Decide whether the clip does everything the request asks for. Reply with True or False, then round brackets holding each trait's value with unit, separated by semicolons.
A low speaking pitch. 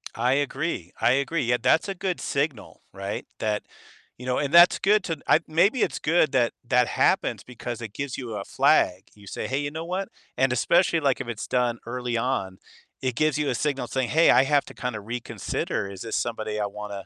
True (125 Hz)